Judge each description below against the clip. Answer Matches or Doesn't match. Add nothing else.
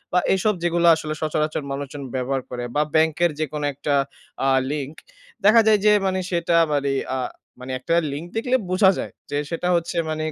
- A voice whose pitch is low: Doesn't match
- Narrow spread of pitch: Doesn't match